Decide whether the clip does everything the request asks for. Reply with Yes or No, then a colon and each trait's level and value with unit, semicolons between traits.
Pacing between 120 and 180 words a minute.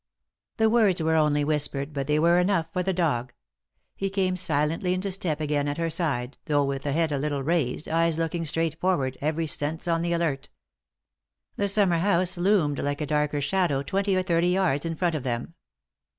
No: average, 195 wpm